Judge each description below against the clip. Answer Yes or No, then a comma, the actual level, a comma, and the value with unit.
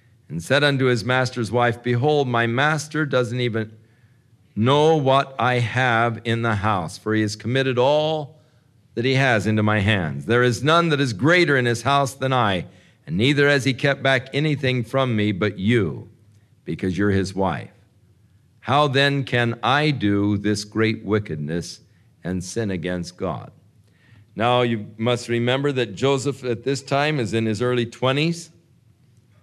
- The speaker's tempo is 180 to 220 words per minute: No, average, 165 wpm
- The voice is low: Yes, low, 120 Hz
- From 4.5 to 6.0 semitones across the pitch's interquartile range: No, average, 3.9 semitones